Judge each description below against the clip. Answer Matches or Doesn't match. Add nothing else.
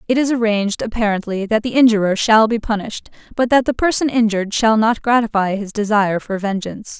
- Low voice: Doesn't match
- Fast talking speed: Doesn't match